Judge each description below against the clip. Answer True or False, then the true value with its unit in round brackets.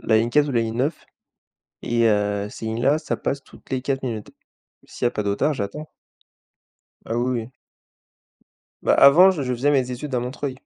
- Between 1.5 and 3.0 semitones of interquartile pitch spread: False (3.7 semitones)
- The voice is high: False (125 Hz)